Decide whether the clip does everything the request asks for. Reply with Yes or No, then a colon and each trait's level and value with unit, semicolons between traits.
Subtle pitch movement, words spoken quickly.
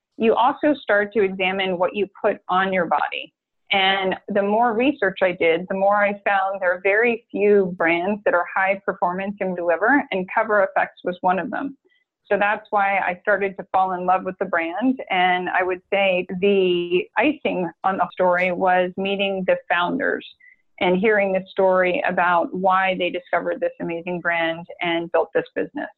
No: narrow, 2.2 semitones; average, 180 wpm